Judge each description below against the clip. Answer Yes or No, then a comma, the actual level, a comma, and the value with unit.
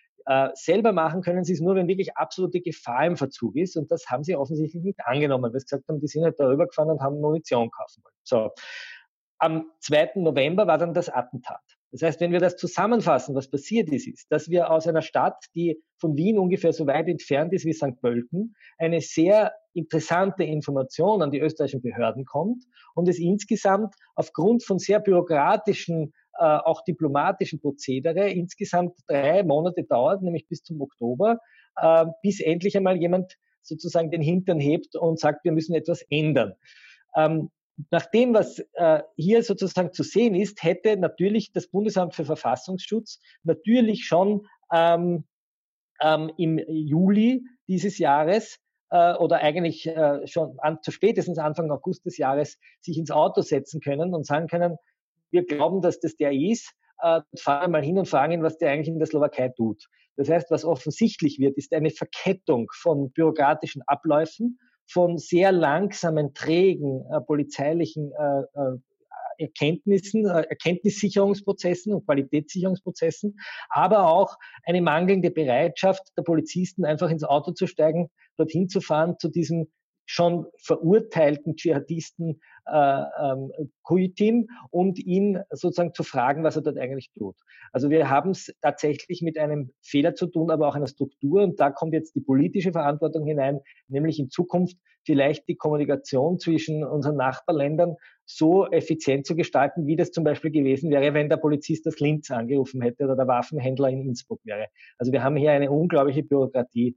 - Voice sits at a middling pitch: Yes, medium, 160 Hz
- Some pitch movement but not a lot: Yes, average, 3.3 semitones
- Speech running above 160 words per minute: No, average, 155 wpm